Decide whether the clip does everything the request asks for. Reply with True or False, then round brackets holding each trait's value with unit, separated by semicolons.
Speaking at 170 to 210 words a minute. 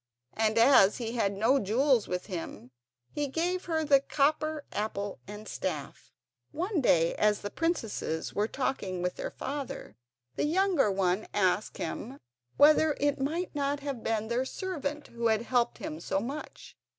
False (160 wpm)